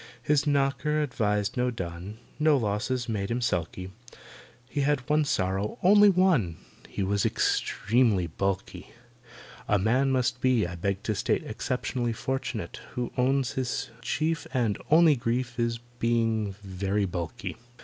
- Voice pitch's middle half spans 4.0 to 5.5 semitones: Yes, average, 4.9 semitones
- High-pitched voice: No, low, 120 Hz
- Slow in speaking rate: Yes, slow, 130 wpm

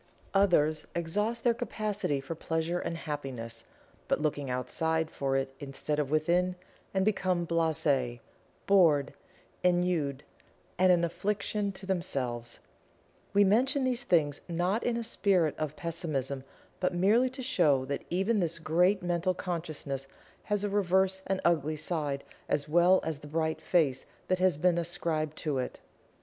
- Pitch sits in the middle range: Yes, medium, 170 Hz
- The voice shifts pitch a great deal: No, average, 4.3 semitones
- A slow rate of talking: No, average, 145 wpm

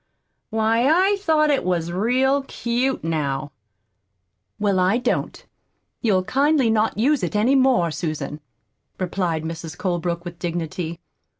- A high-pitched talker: Yes, high, 200 Hz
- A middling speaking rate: No, slow, 125 wpm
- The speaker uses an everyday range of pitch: No, wide, 7.2 semitones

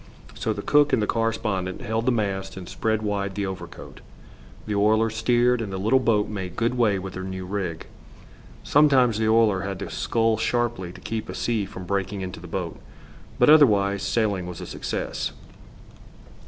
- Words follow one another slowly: No, average, 180 wpm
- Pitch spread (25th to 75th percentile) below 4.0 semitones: Yes, average, 3.1 semitones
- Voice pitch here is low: Yes, low, 105 Hz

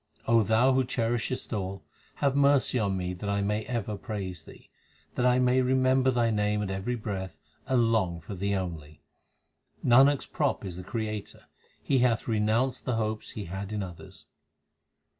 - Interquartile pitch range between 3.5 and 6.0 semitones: Yes, average, 4.3 semitones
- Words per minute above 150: Yes, average, 170 wpm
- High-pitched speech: No, low, 110 Hz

